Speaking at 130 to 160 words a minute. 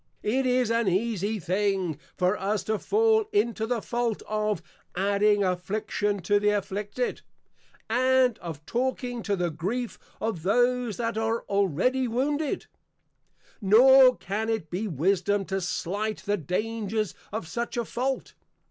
Yes: average, 140 wpm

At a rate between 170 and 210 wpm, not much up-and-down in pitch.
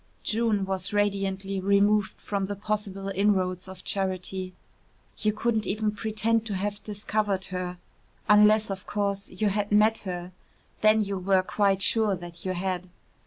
No: average, 150 wpm; narrow, 1.9 semitones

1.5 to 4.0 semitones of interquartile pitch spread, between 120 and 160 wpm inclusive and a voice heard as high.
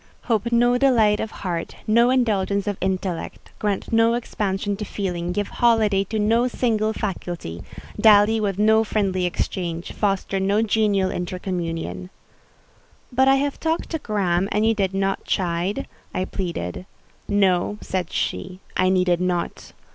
Yes: average, 3.2 semitones; average, 140 wpm; high, 200 Hz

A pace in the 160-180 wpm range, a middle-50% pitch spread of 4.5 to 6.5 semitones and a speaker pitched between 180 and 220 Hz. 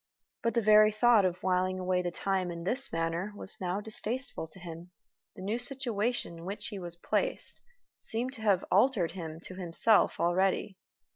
No: average, 175 wpm; average, 3.9 semitones; high, 190 Hz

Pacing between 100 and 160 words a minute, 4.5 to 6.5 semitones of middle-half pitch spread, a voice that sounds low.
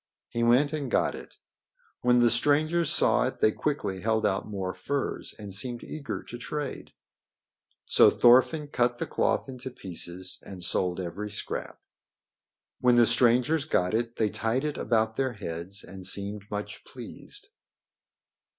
Yes: average, 150 wpm; average, 4.8 semitones; low, 115 Hz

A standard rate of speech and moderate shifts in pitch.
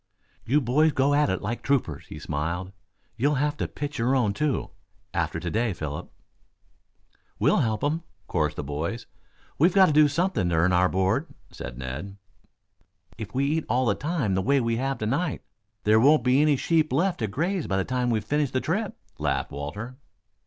No: average, 190 wpm; wide, 7.7 semitones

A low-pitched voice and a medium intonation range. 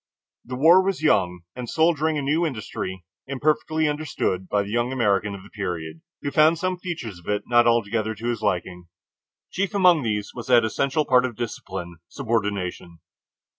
No: low, 120 Hz; wide, 7.1 semitones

